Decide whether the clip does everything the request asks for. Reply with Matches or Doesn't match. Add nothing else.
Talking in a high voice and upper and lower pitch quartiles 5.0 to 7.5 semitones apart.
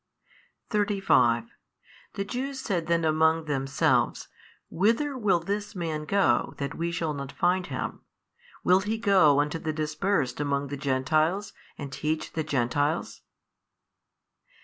Doesn't match